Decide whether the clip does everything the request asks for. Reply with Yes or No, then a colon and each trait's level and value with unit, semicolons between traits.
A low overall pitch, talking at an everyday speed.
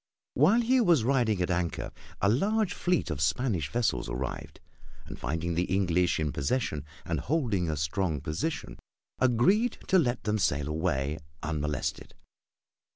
Yes: very low, 95 Hz; average, 145 wpm